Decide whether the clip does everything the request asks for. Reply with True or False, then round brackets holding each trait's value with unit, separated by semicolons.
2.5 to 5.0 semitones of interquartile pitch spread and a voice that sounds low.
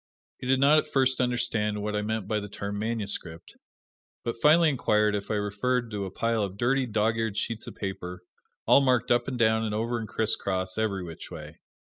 True (2.9 semitones; 110 Hz)